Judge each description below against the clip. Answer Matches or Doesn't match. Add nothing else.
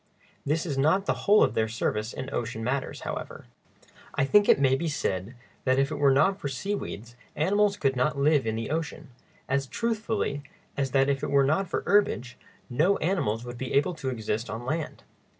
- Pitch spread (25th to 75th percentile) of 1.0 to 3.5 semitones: Doesn't match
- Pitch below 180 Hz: Matches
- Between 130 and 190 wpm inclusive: Doesn't match